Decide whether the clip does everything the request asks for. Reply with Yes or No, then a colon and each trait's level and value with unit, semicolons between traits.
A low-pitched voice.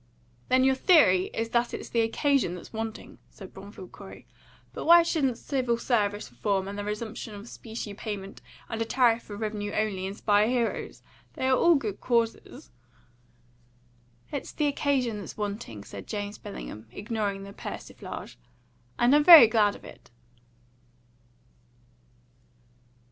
No: high, 220 Hz